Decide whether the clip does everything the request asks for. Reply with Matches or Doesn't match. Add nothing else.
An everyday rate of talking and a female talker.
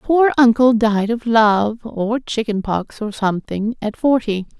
Matches